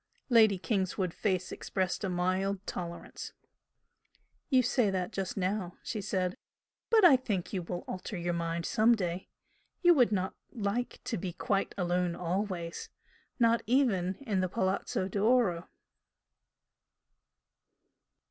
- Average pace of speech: No, slow, 130 wpm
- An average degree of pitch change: Yes, average, 3.4 semitones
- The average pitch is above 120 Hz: Yes, high, 190 Hz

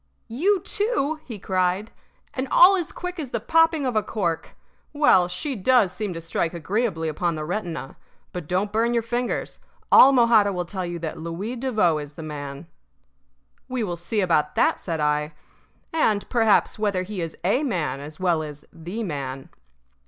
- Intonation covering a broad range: Yes, wide, 6.4 semitones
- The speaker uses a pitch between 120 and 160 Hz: No, high, 190 Hz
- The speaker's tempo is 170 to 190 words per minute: Yes, average, 175 wpm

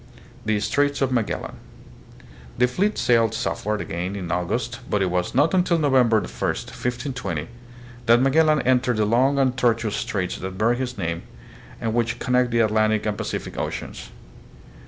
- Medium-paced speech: Yes, average, 160 wpm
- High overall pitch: No, low, 115 Hz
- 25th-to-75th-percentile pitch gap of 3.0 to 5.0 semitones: Yes, average, 3.7 semitones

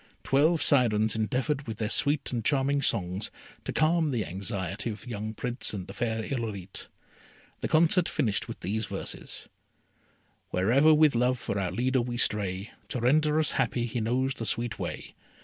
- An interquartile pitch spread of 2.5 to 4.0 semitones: No, average, 4.7 semitones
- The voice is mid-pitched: No, low, 120 Hz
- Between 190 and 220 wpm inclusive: No, average, 170 wpm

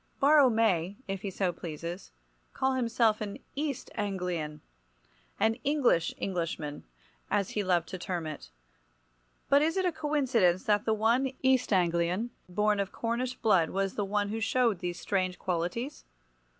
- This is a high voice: Yes, high, 200 Hz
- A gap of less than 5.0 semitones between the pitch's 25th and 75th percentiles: No, wide, 5.4 semitones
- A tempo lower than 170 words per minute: Yes, average, 145 wpm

